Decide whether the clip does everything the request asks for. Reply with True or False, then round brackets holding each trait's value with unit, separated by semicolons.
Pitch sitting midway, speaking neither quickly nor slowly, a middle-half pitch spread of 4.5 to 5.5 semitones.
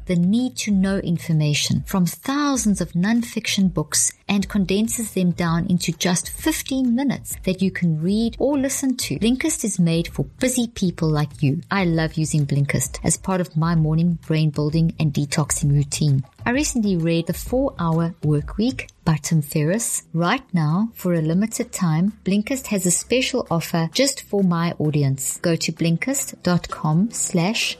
True (180 Hz; 165 wpm; 5.1 semitones)